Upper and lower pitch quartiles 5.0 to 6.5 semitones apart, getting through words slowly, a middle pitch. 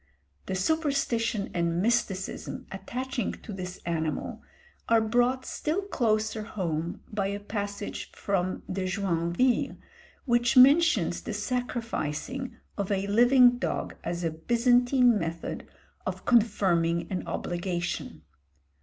No: average, 5.3 semitones; slow, 110 wpm; high, 210 Hz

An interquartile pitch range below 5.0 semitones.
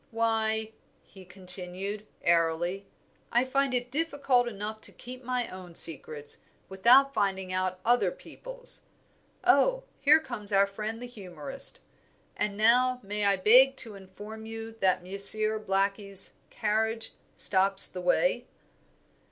Yes: average, 4.3 semitones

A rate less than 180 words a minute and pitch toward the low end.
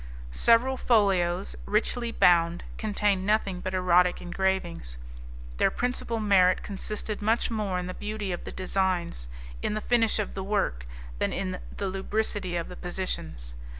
No: average, 150 wpm; high, 190 Hz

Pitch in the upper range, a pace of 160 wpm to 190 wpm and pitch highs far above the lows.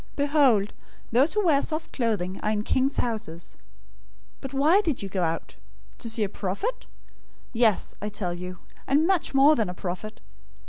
Yes: high, 230 Hz; average, 175 wpm; wide, 6.7 semitones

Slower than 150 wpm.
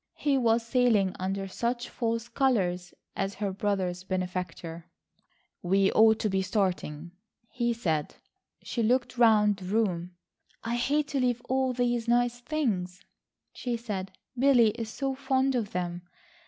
Yes: average, 140 wpm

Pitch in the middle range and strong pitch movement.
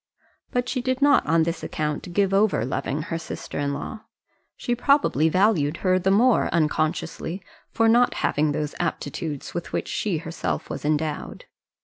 Yes: medium, 165 Hz; wide, 6.0 semitones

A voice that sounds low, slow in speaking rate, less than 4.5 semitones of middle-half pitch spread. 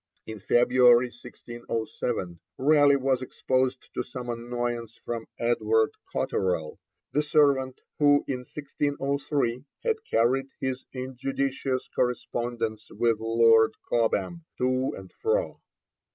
Yes: low, 125 Hz; slow, 105 wpm; average, 2.7 semitones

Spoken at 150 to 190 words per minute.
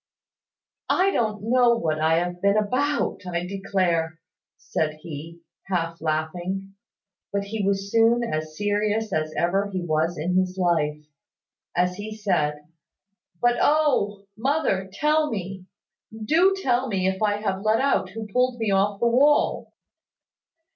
No: average, 140 wpm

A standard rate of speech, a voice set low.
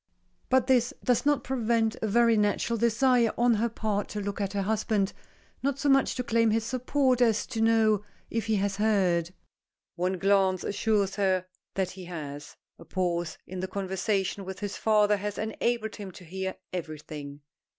No: average, 175 wpm; high, 210 Hz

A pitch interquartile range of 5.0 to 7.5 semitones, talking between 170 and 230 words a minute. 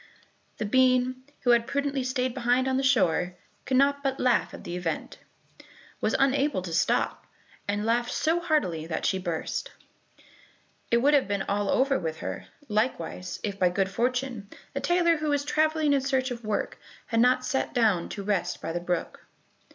Yes: wide, 5.6 semitones; average, 180 wpm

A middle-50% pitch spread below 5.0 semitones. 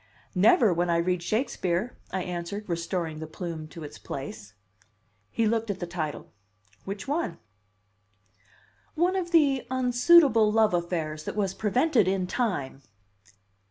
No: average, 5.3 semitones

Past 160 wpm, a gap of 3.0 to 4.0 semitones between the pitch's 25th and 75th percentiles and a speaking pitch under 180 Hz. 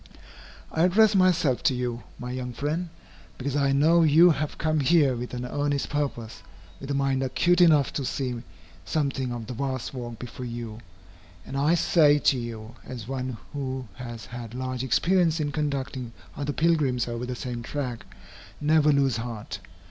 Yes: average, 170 wpm; average, 3.4 semitones; low, 135 Hz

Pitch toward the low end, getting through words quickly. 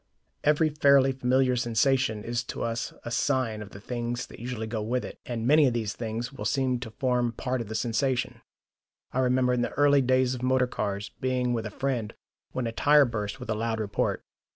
Yes: low, 125 Hz; fast, 210 wpm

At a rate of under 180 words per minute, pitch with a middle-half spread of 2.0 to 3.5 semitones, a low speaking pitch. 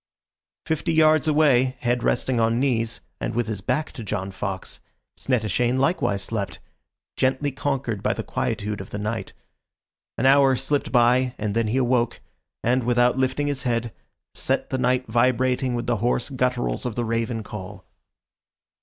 Yes: average, 160 wpm; narrow, 2.5 semitones; low, 125 Hz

